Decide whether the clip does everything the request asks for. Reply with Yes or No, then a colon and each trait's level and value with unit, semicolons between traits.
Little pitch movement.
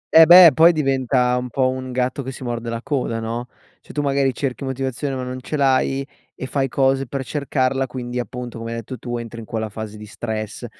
Yes: narrow, 2.3 semitones